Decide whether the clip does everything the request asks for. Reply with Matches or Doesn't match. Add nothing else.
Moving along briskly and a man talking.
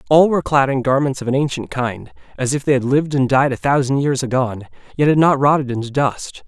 Matches